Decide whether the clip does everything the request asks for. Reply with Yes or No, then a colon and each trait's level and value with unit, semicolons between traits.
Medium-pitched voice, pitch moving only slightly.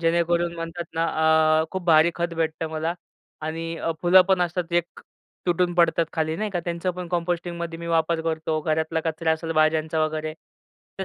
Yes: medium, 165 Hz; narrow, 1.4 semitones